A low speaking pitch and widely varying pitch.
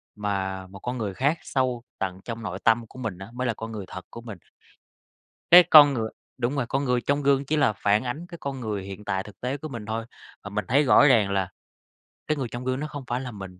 No: low, 115 Hz; average, 4.8 semitones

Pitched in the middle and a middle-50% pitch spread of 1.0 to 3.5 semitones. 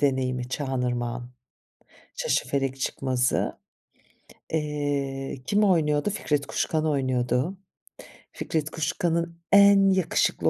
No: medium, 145 Hz; average, 4.4 semitones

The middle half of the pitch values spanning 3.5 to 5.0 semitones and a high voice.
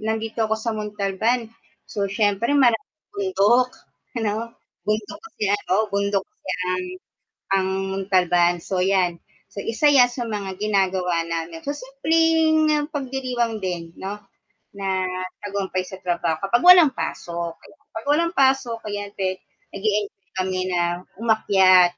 Yes: average, 4.3 semitones; high, 205 Hz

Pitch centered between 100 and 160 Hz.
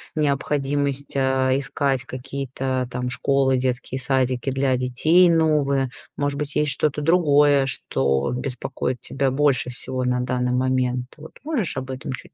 Yes: low, 135 Hz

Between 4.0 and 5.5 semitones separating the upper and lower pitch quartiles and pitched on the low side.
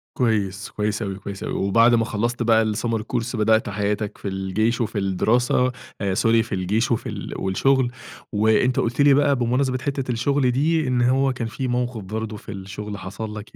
No: average, 3.2 semitones; low, 115 Hz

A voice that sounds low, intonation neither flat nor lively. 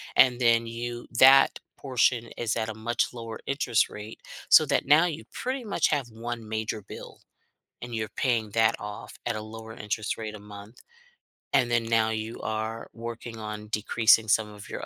No: low, 115 Hz; narrow, 1.7 semitones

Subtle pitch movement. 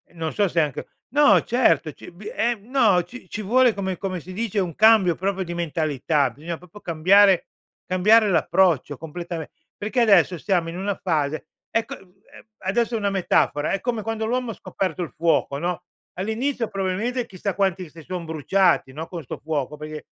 No: average, 4.4 semitones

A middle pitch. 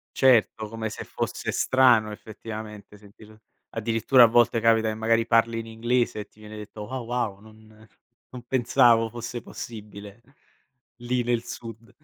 No: low, 115 Hz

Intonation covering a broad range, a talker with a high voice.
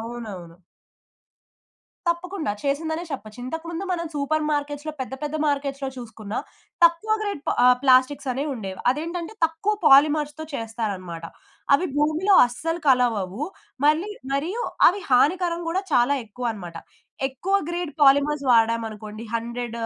Yes: wide, 5.7 semitones; very high, 280 Hz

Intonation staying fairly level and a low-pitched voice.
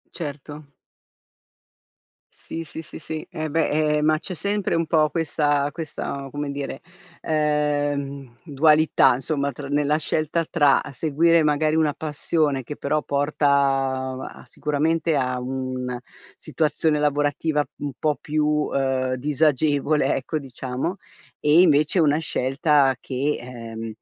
No: narrow, 2.0 semitones; medium, 150 Hz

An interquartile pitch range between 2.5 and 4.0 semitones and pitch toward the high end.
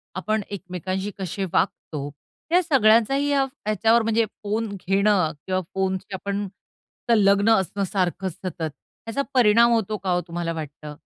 Yes: average, 3.3 semitones; high, 200 Hz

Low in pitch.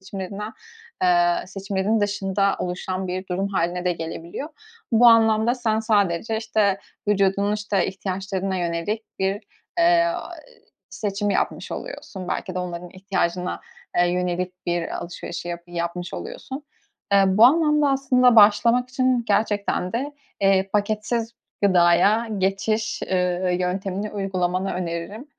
No: high, 195 Hz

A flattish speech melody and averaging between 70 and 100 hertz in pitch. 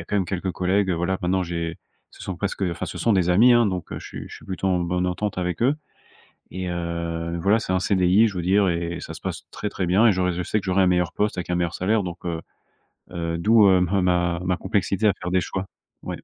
Yes: narrow, 2.0 semitones; very low, 90 Hz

